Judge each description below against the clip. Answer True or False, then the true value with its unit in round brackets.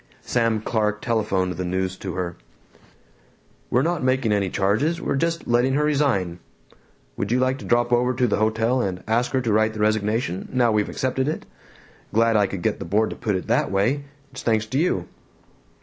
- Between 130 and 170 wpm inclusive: False (195 wpm)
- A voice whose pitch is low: True (110 Hz)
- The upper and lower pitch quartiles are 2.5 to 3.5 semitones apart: False (4.1 semitones)